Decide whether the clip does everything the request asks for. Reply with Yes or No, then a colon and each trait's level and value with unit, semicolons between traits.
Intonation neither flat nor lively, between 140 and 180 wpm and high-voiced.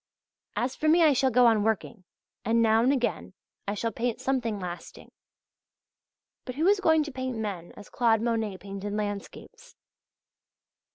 Yes: average, 4.0 semitones; average, 160 wpm; high, 230 Hz